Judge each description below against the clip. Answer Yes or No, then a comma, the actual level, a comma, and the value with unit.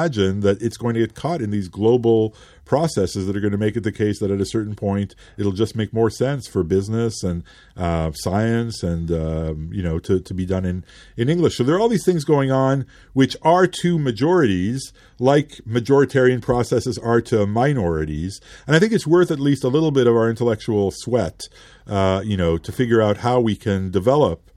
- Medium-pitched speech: No, low, 110 Hz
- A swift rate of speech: Yes, fast, 210 wpm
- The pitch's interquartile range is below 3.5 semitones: No, average, 5.0 semitones